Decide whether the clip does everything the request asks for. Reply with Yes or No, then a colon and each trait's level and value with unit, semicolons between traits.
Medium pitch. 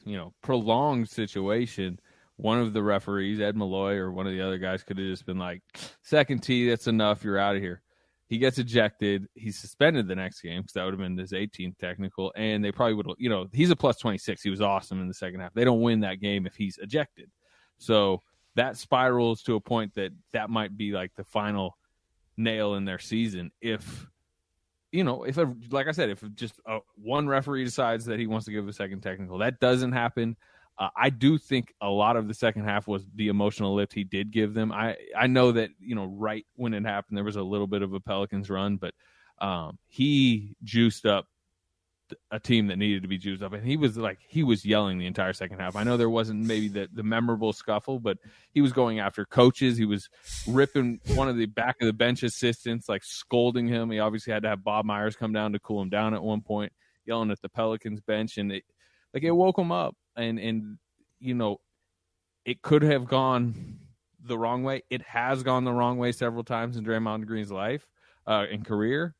No: low, 110 Hz